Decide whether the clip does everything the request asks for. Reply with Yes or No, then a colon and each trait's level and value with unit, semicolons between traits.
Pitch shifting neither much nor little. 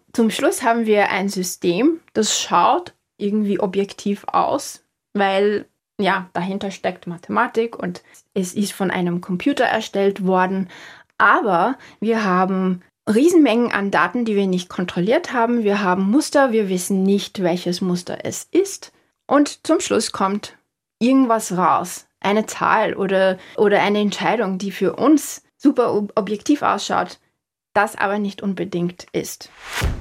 Yes: average, 3.4 semitones